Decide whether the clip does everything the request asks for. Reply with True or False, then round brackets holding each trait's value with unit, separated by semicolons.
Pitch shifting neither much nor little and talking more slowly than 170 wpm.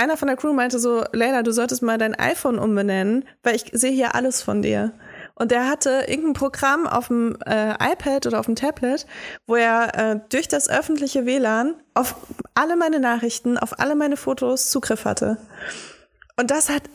False (3.4 semitones; 190 wpm)